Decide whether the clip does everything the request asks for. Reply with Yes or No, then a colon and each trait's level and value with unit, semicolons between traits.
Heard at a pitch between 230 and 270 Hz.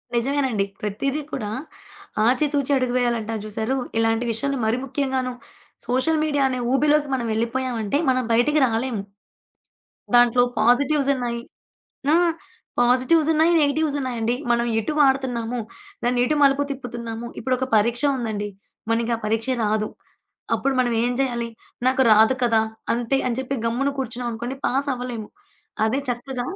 Yes: high, 245 Hz